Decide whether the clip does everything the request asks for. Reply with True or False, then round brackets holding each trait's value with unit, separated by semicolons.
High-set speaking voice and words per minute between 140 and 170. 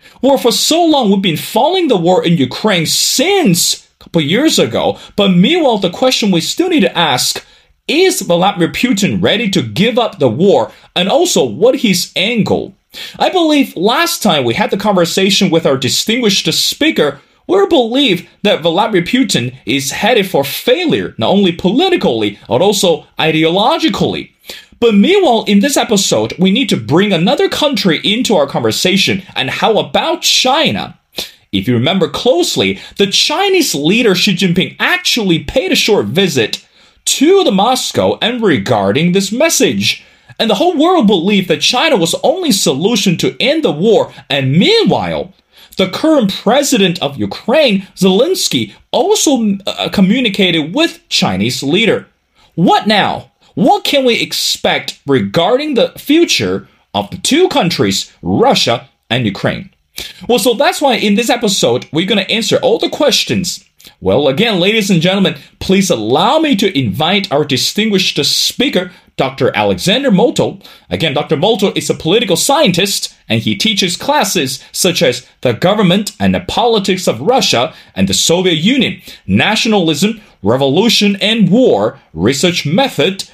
True (195 Hz; 150 wpm)